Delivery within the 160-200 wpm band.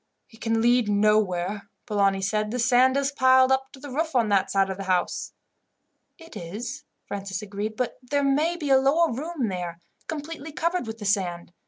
Yes: average, 190 wpm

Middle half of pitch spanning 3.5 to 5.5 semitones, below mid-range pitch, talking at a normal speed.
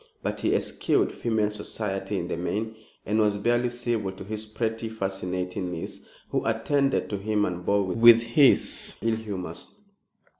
No: average, 2.8 semitones; low, 105 Hz; average, 155 wpm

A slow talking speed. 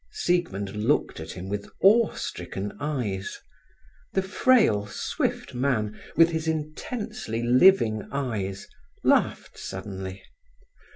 Yes: slow, 105 wpm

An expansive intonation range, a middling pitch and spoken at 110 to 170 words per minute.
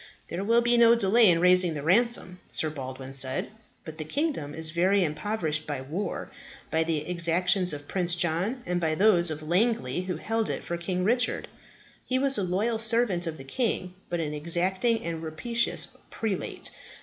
No: wide, 5.7 semitones; medium, 180 Hz; average, 180 wpm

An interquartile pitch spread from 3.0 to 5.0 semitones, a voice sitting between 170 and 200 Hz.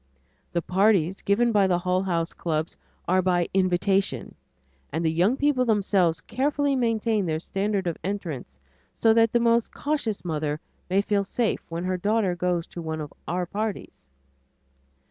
Yes: average, 4.3 semitones; high, 190 Hz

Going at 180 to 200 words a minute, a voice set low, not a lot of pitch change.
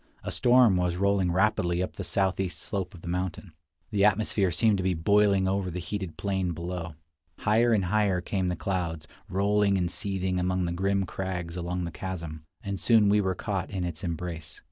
Yes: average, 190 wpm; very low, 95 Hz; narrow, 2.2 semitones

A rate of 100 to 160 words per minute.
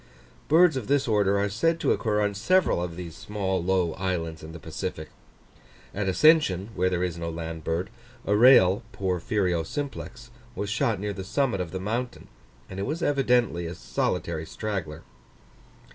No: average, 170 wpm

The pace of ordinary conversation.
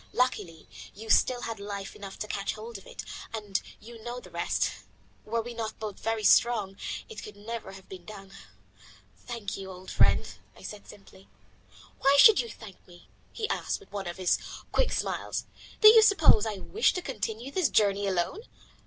Yes: average, 190 wpm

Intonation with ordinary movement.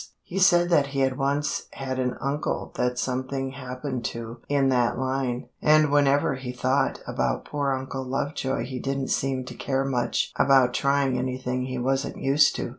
No: narrow, 1.5 semitones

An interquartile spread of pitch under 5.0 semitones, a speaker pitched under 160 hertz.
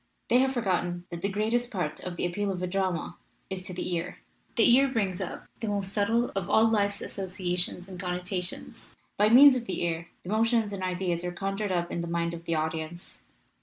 No: average, 3.2 semitones; medium, 185 Hz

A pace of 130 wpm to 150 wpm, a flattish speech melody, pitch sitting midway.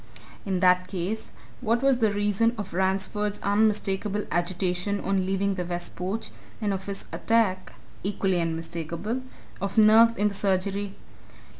No: average, 140 wpm; narrow, 2.3 semitones; high, 195 Hz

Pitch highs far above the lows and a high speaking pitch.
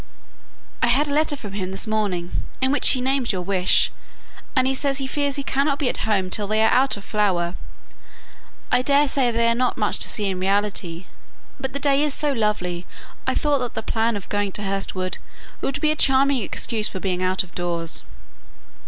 Yes: wide, 5.8 semitones; high, 220 Hz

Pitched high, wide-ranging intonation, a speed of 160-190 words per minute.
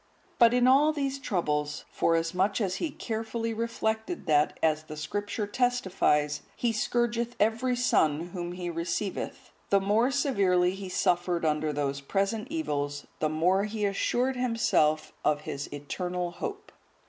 No: high, 195 Hz; wide, 6.6 semitones; average, 140 wpm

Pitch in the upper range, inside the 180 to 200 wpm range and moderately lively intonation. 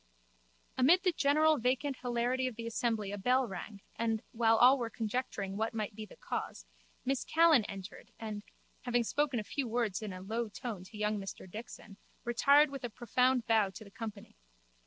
Yes: high, 230 Hz; average, 185 wpm; average, 3.4 semitones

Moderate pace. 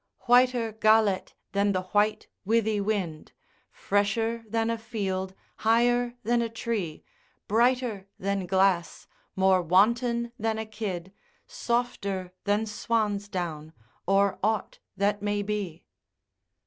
No: slow, 115 wpm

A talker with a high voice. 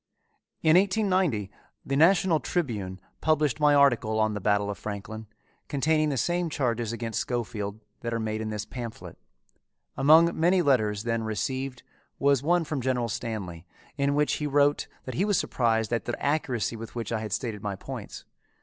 No: low, 120 Hz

